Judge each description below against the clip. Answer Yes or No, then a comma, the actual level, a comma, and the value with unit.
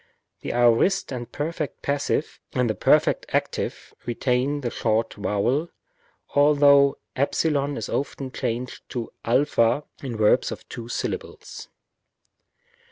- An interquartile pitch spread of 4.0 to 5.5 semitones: No, average, 3.5 semitones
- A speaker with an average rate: No, slow, 115 wpm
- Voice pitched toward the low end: Yes, low, 130 Hz